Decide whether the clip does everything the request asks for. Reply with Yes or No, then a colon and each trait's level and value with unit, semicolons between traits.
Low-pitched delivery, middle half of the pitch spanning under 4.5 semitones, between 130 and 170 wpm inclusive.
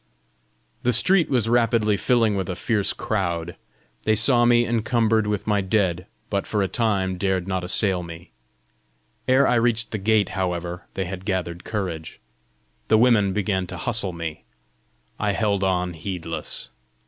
Yes: low, 100 Hz; average, 3.7 semitones; average, 155 wpm